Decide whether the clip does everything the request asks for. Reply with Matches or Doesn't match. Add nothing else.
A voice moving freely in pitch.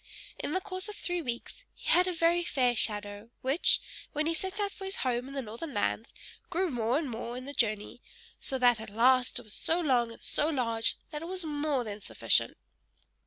Matches